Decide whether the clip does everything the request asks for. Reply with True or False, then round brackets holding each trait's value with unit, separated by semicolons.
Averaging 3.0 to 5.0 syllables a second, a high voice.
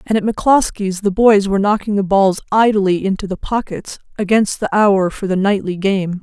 False (5.2 syllables/s; 200 Hz)